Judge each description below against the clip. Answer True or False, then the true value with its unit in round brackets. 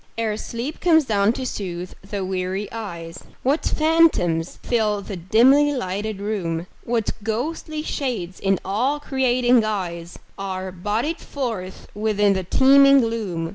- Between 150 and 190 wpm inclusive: False (135 wpm)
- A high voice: True (215 Hz)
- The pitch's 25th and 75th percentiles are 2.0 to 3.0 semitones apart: False (5.5 semitones)